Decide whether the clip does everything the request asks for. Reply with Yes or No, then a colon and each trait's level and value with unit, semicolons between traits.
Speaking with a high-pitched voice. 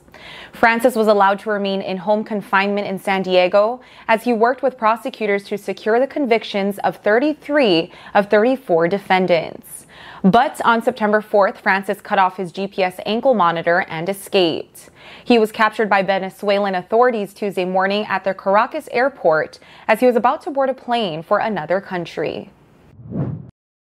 Yes: high, 205 Hz